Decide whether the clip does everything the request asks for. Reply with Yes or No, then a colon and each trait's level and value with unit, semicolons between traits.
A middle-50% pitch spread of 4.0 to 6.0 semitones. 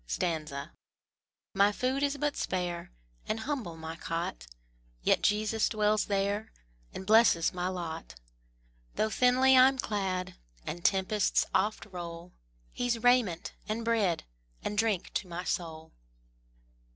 Yes: average, 4.6 semitones